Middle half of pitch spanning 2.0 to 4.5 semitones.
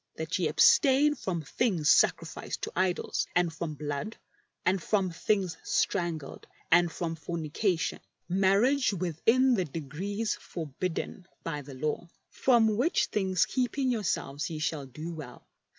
No: average, 5.1 semitones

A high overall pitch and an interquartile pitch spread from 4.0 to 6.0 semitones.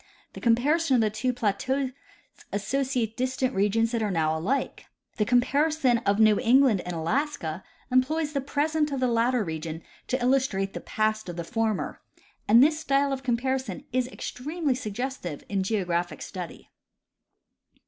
Yes: high, 245 Hz; average, 4.9 semitones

